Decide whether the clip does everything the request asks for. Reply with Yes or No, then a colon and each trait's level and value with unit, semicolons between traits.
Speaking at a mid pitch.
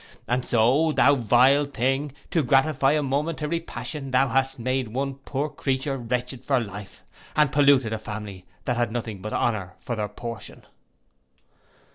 No: low, 130 Hz